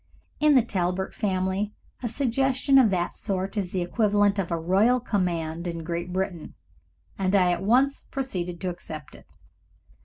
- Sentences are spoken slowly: No, average, 160 wpm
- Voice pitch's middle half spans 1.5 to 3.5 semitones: No, average, 4.3 semitones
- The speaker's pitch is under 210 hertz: Yes, high, 190 Hz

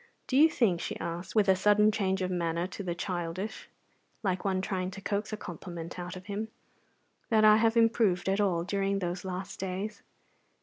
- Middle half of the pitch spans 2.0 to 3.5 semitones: Yes, average, 2.7 semitones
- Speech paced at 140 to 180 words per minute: No, average, 190 wpm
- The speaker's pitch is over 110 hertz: Yes, high, 190 Hz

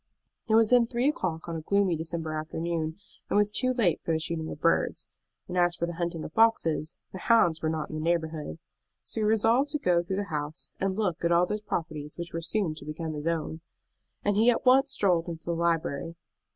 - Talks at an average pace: No, fast, 230 wpm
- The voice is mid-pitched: Yes, medium, 170 Hz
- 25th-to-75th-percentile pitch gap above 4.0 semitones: Yes, average, 4.5 semitones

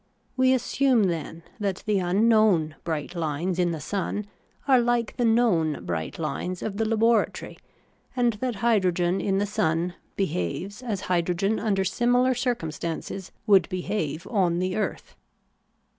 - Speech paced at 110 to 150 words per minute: Yes, average, 140 wpm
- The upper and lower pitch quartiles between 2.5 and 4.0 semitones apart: No, average, 4.8 semitones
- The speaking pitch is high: Yes, high, 195 Hz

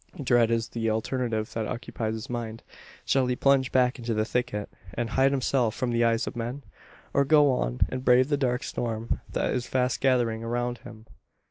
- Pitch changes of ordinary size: No, narrow, 2.1 semitones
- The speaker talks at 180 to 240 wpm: Yes, average, 195 wpm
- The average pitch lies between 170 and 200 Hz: No, low, 120 Hz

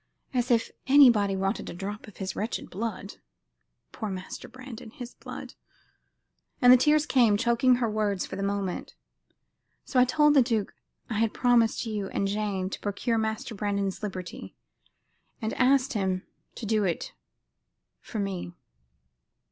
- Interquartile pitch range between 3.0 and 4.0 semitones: Yes, average, 3.7 semitones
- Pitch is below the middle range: No, high, 215 Hz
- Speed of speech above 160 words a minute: No, average, 155 wpm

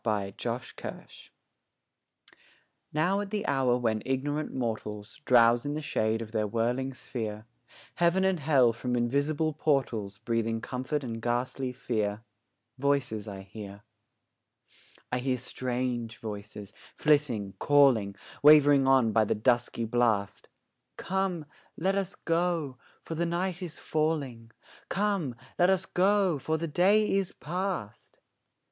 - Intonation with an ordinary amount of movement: No, wide, 5.8 semitones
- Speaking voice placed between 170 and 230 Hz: No, low, 130 Hz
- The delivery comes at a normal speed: No, slow, 125 wpm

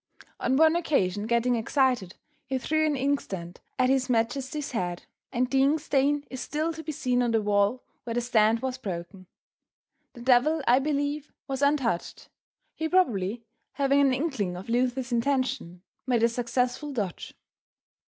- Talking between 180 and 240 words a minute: No, average, 160 wpm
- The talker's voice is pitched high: Yes, very high, 255 Hz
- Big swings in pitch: No, average, 3.7 semitones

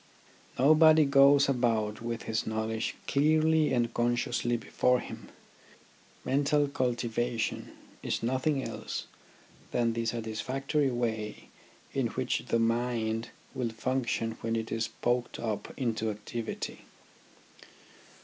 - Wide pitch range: No, average, 3.1 semitones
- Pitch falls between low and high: No, low, 120 Hz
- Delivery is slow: Yes, slow, 110 wpm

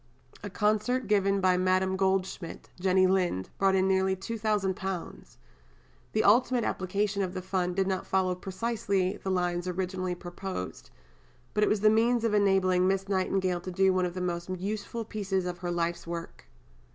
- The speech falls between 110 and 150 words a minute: No, average, 165 wpm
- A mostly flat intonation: Yes, narrow, 1.7 semitones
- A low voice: No, high, 190 Hz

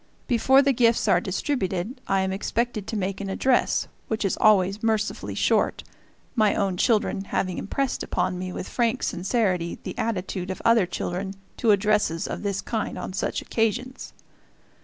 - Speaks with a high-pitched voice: Yes, high, 205 Hz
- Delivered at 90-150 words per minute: No, average, 160 wpm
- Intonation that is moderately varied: Yes, average, 3.5 semitones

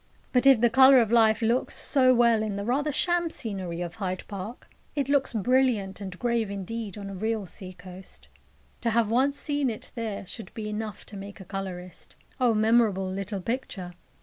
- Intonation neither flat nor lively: Yes, average, 4.0 semitones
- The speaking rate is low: No, average, 190 wpm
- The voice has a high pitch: Yes, high, 220 Hz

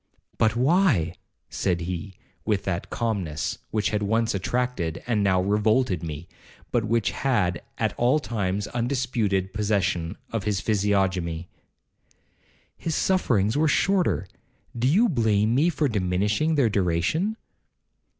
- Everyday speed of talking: No, slow, 120 wpm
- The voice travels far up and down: No, average, 5.0 semitones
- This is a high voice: No, low, 105 Hz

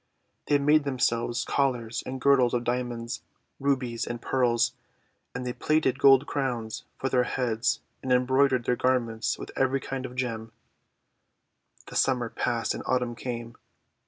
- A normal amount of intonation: No, narrow, 2.1 semitones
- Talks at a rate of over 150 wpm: No, average, 145 wpm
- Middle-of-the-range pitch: No, low, 125 Hz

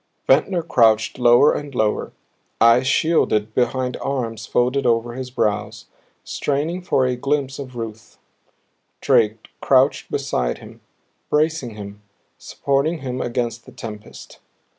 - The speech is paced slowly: Yes, slow, 120 wpm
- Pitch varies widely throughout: No, average, 3.4 semitones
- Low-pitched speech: Yes, low, 125 Hz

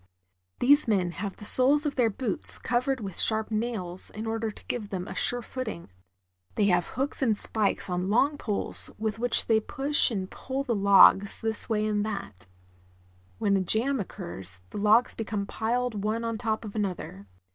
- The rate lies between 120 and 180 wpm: No, average, 190 wpm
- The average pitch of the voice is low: No, high, 215 Hz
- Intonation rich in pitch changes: No, average, 3.3 semitones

